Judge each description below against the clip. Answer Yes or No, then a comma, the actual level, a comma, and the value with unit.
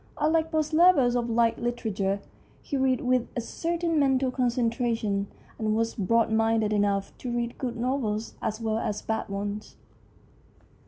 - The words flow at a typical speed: Yes, average, 155 wpm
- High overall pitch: Yes, high, 235 Hz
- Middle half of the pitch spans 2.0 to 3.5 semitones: Yes, average, 3.2 semitones